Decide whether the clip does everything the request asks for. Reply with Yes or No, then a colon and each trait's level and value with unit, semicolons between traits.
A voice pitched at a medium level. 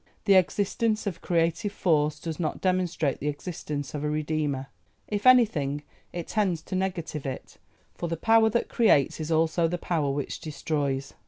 Yes: medium, 165 Hz